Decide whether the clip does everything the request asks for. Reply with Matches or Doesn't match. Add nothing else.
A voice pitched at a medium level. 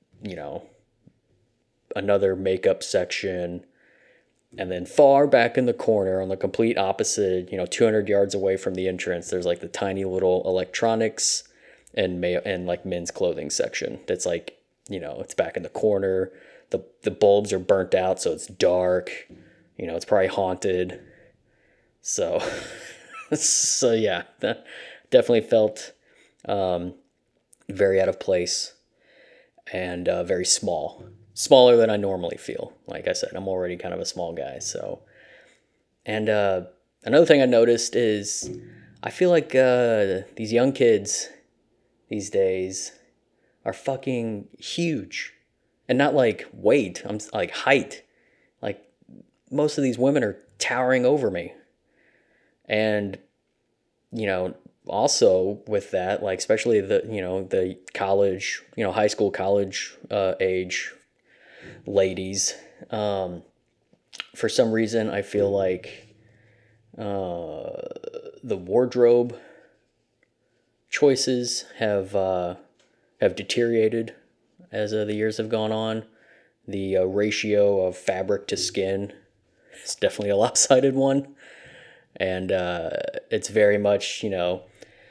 Doesn't match